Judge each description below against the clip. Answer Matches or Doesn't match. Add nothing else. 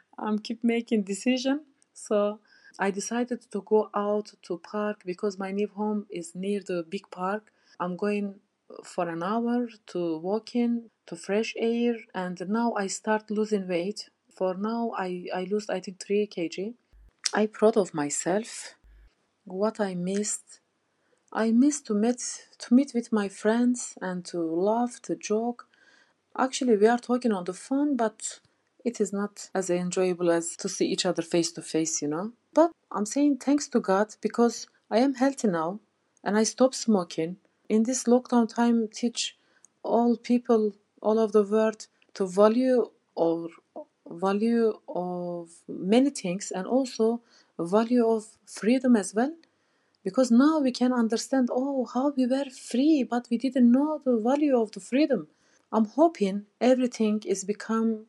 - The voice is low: Doesn't match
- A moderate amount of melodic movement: Matches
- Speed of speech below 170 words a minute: Matches